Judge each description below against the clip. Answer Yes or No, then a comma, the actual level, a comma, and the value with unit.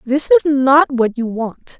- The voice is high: Yes, very high, 250 Hz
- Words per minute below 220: Yes, average, 200 wpm